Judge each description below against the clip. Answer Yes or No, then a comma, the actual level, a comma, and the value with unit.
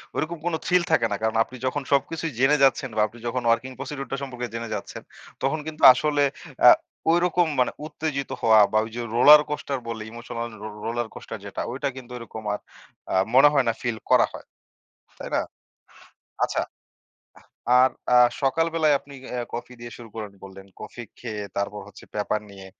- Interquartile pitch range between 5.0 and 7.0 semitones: No, average, 4.2 semitones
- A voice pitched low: Yes, low, 125 Hz